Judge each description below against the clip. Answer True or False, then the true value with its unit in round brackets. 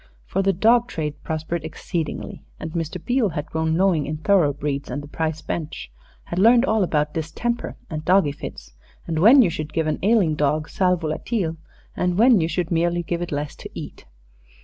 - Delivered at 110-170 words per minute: False (190 wpm)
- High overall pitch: False (165 Hz)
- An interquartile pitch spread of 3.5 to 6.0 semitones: True (3.9 semitones)